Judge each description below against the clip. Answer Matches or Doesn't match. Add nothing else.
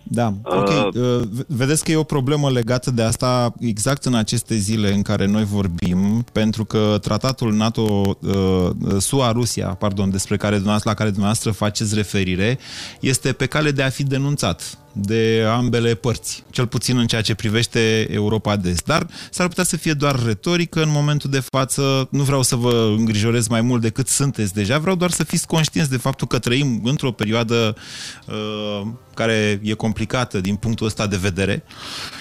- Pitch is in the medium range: Doesn't match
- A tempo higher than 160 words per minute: Matches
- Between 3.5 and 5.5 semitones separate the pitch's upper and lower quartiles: Matches